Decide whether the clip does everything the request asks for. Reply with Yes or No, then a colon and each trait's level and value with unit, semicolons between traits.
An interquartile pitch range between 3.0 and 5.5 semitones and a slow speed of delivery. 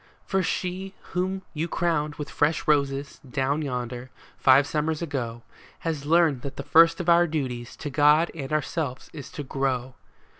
No: average, 3.6 semitones; average, 165 wpm